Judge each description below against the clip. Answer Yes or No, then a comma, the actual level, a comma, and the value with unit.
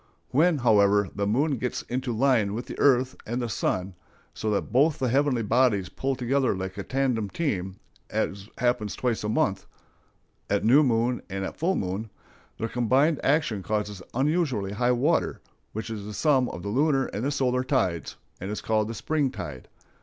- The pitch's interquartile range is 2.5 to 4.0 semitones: No, average, 4.7 semitones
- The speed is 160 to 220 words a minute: Yes, average, 170 wpm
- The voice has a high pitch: No, low, 120 Hz